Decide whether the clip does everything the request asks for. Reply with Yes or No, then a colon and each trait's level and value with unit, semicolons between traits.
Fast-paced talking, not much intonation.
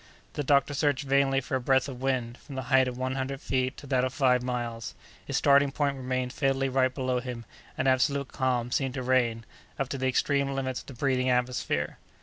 Yes: fast, 215 wpm; narrow, 1.3 semitones